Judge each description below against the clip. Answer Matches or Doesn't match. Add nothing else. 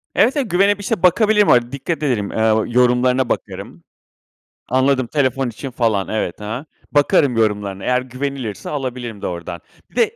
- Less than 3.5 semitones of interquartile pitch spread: Doesn't match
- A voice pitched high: Doesn't match